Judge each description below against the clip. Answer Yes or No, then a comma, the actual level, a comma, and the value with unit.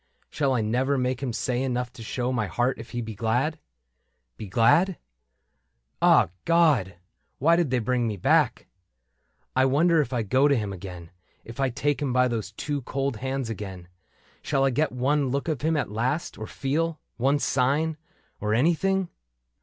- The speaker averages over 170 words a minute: Yes, average, 185 wpm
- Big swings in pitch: No, average, 4.1 semitones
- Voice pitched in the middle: No, low, 130 Hz